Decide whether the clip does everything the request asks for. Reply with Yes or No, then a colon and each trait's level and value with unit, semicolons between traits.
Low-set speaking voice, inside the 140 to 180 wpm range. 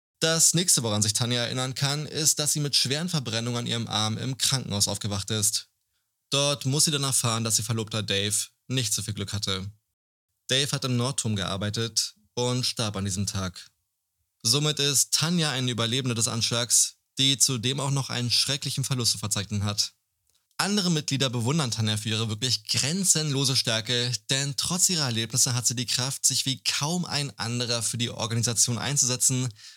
Yes: low, 120 Hz; average, 175 wpm